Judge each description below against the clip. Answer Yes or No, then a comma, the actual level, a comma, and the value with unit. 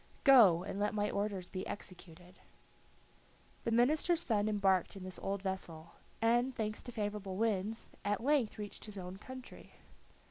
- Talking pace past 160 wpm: No, average, 150 wpm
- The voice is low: No, high, 205 Hz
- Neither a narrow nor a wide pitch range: Yes, average, 3.2 semitones